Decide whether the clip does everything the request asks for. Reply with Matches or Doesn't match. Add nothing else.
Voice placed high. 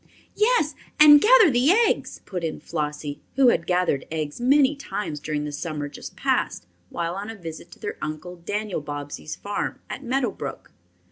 Doesn't match